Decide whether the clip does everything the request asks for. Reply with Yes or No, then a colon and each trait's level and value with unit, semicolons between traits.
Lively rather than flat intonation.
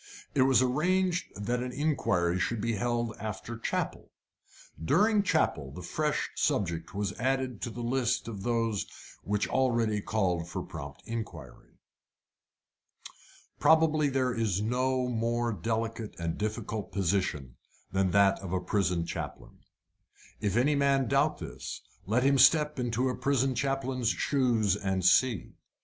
No: average, 4.9 semitones